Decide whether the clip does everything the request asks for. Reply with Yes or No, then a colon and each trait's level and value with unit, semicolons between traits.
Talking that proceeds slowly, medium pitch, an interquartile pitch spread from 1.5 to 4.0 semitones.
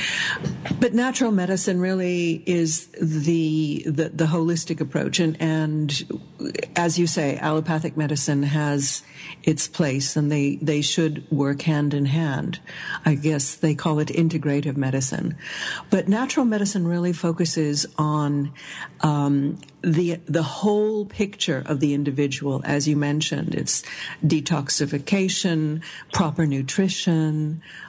Yes: slow, 120 wpm; medium, 155 Hz; average, 2.7 semitones